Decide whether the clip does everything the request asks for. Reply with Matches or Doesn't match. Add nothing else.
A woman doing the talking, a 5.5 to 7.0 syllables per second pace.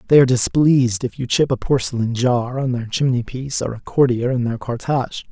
Doesn't match